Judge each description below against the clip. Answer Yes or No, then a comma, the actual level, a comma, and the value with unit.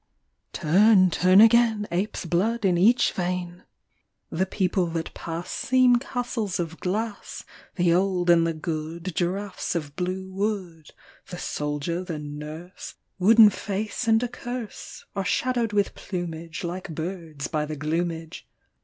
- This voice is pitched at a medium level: Yes, medium, 180 Hz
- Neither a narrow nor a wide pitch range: Yes, average, 3.8 semitones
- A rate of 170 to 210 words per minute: No, slow, 135 wpm